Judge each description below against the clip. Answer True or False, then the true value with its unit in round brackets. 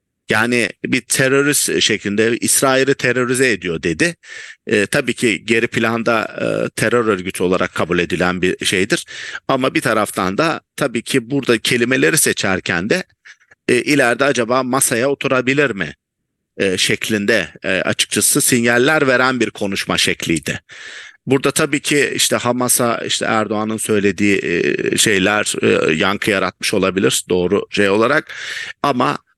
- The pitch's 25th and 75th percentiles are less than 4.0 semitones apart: True (3.5 semitones)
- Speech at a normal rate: False (130 wpm)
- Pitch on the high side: False (120 Hz)